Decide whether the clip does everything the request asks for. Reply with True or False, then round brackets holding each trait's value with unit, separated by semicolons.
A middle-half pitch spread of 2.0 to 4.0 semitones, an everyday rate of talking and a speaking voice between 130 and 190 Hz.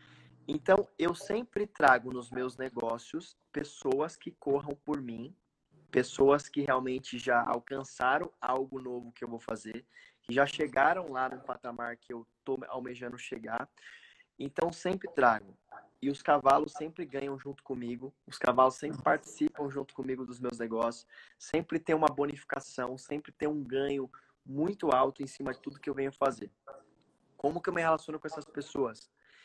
True (3.1 semitones; 160 wpm; 135 Hz)